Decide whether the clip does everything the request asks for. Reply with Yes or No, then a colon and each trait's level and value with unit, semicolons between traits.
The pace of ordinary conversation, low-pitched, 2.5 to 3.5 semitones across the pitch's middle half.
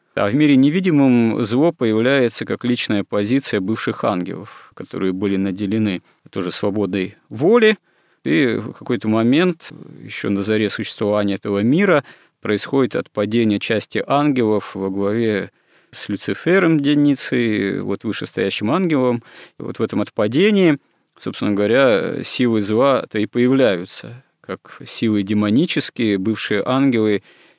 No: average, 120 wpm; low, 110 Hz; average, 4.6 semitones